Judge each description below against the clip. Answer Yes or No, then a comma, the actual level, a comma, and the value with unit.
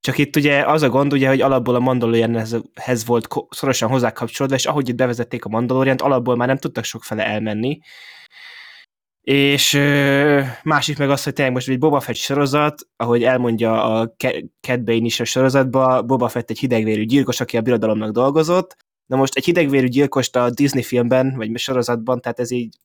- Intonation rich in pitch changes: No, average, 2.9 semitones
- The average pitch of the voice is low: Yes, low, 130 Hz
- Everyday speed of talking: No, fast, 175 wpm